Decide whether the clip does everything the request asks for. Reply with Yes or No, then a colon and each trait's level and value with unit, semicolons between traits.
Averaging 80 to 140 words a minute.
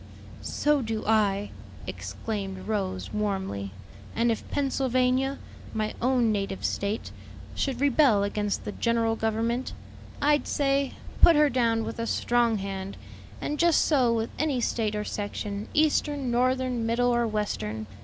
Yes: slow, 135 wpm